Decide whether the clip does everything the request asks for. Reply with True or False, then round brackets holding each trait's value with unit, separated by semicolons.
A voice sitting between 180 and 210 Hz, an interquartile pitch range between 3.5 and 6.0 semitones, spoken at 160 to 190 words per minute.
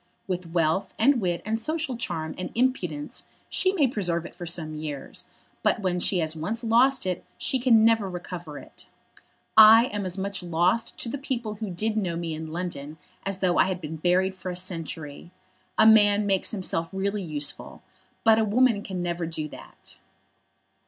True (185 Hz; 4.5 semitones; 185 wpm)